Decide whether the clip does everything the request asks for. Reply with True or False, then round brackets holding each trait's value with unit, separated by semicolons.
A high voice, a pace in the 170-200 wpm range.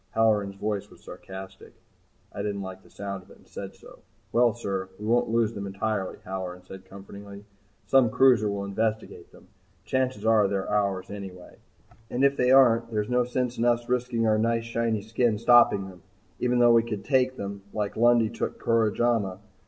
False (110 Hz; 185 wpm)